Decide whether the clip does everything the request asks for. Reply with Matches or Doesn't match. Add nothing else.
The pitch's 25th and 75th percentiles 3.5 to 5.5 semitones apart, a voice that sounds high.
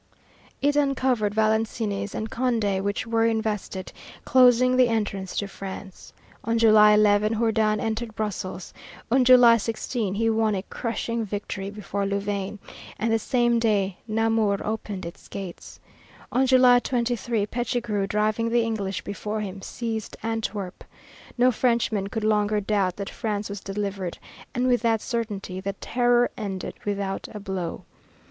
Doesn't match